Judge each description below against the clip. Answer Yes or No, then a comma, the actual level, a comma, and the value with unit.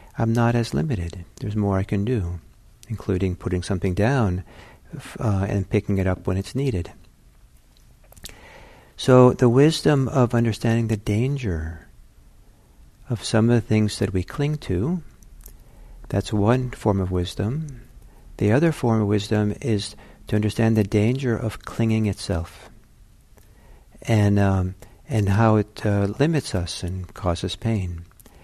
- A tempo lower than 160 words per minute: Yes, average, 140 wpm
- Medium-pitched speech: No, low, 105 Hz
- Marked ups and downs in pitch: No, average, 3.7 semitones